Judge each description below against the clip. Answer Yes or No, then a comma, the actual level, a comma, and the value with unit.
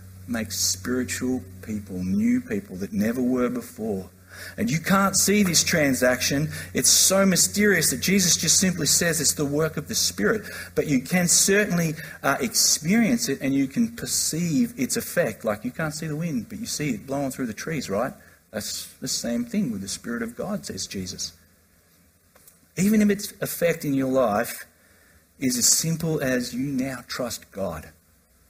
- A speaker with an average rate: Yes, average, 175 wpm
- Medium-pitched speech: Yes, medium, 150 Hz